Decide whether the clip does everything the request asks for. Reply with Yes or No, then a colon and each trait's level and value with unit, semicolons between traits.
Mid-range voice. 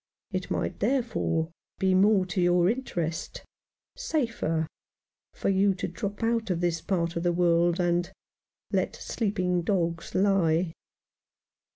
Yes: medium, 180 Hz